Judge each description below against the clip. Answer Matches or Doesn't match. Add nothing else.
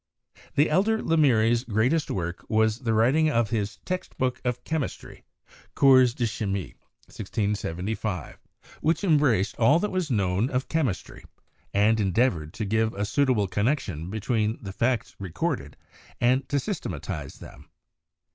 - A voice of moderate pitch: Doesn't match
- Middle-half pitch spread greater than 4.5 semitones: Matches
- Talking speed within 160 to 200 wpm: Doesn't match